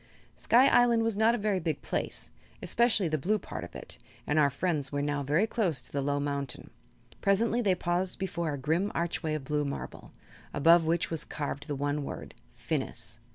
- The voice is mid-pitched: Yes, medium, 165 Hz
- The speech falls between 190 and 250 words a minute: Yes, average, 195 wpm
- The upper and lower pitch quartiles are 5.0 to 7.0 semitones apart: Yes, wide, 5.6 semitones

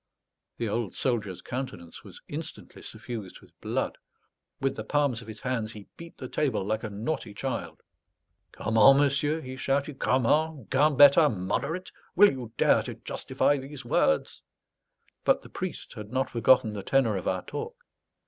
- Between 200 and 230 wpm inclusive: No, average, 160 wpm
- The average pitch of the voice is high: No, low, 130 Hz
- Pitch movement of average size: Yes, average, 4.4 semitones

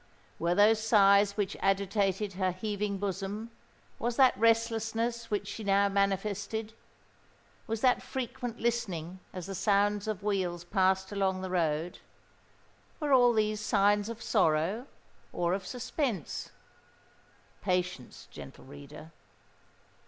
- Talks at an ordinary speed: No, slow, 110 wpm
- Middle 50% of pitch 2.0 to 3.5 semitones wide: Yes, average, 3.0 semitones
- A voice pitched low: No, high, 200 Hz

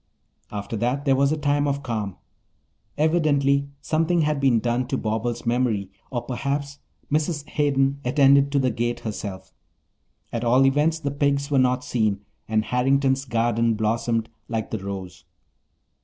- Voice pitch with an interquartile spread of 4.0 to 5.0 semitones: No, average, 3.6 semitones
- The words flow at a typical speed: Yes, average, 150 wpm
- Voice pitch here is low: Yes, low, 130 Hz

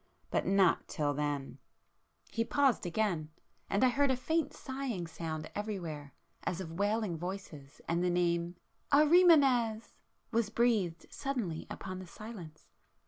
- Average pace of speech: No, slow, 130 wpm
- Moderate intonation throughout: No, wide, 6.2 semitones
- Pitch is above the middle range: Yes, high, 195 Hz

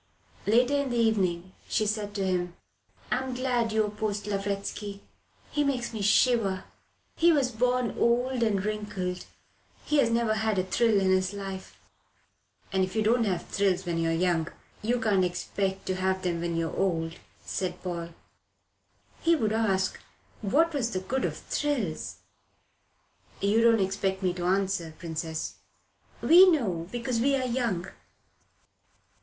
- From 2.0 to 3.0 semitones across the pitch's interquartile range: No, average, 4.1 semitones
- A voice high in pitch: Yes, high, 205 Hz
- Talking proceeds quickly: No, average, 150 wpm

